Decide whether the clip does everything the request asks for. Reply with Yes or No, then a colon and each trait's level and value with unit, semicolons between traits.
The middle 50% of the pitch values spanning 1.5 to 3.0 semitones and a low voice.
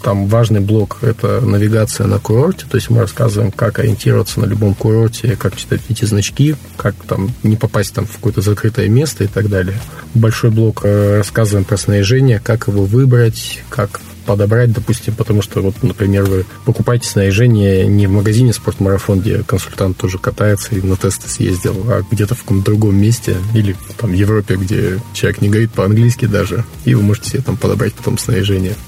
Yes: narrow, 2.6 semitones; low, 110 Hz